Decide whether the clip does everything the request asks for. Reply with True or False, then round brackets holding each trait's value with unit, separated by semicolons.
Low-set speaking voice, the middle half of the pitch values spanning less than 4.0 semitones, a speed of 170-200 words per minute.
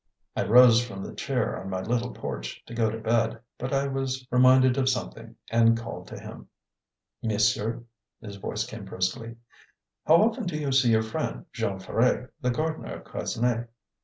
True (115 Hz; 2.7 semitones; 175 wpm)